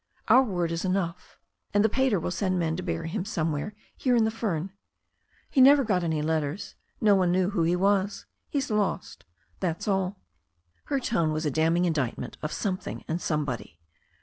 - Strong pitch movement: No, average, 4.1 semitones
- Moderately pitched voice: Yes, medium, 180 Hz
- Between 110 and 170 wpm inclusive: No, average, 180 wpm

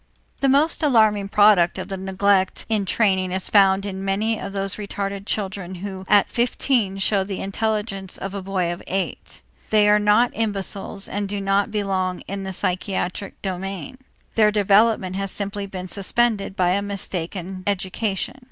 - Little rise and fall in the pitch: Yes, narrow, 1.6 semitones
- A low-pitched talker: No, high, 195 Hz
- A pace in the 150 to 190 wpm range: Yes, average, 160 wpm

